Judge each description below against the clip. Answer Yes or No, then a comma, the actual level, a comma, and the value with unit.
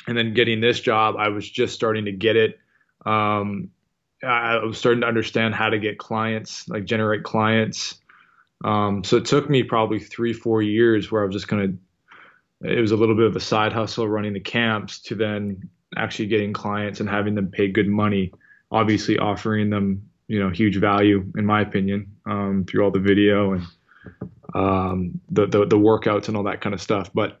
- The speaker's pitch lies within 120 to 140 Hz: No, low, 105 Hz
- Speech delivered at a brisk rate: No, average, 195 wpm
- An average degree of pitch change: No, narrow, 1.6 semitones